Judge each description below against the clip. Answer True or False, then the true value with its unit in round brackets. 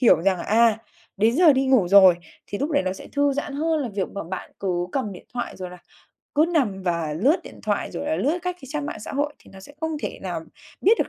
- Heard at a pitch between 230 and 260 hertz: True (235 Hz)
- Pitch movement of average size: False (7.2 semitones)